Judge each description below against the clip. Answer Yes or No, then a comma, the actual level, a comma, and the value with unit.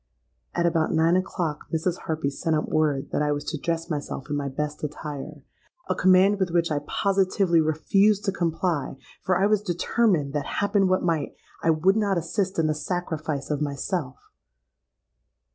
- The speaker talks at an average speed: Yes, average, 170 wpm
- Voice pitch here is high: No, medium, 165 Hz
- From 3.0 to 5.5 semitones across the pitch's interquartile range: Yes, average, 3.8 semitones